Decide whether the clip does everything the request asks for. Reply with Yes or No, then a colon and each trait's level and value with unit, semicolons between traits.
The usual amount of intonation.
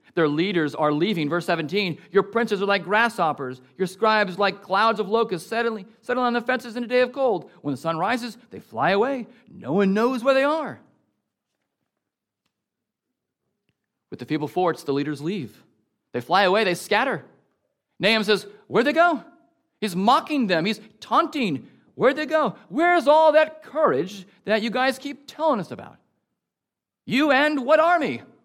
No: wide, 6.5 semitones